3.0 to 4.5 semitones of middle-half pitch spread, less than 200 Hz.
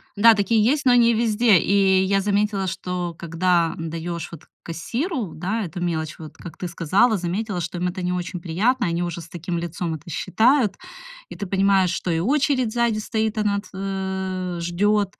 Yes: average, 3.8 semitones; high, 190 Hz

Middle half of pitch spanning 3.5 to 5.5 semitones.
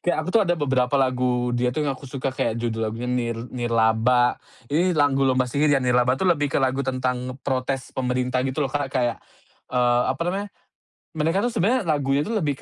No: average, 2.8 semitones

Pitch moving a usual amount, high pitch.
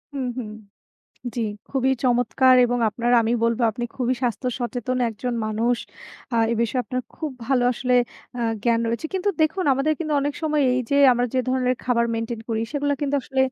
No: narrow, 2.3 semitones; very high, 250 Hz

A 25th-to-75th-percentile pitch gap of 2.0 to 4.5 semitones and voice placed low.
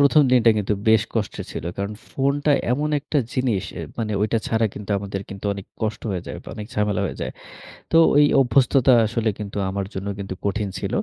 Yes: average, 4.2 semitones; low, 110 Hz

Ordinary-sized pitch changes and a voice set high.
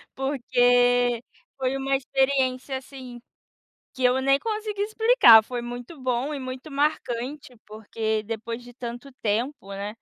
No: narrow, 2.3 semitones; very high, 255 Hz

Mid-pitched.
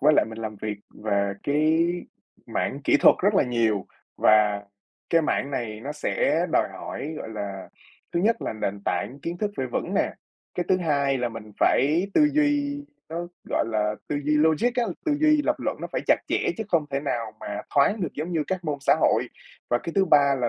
Yes: medium, 145 Hz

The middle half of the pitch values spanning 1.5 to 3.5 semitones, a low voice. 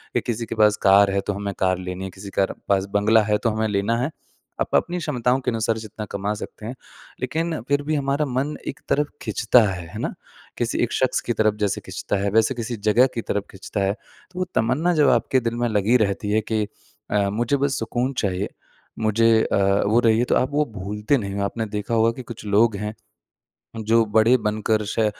Yes: average, 3.2 semitones; low, 110 Hz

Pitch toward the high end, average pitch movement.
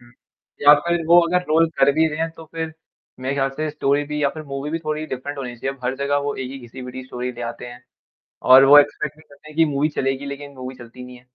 No: medium, 140 Hz; average, 3.0 semitones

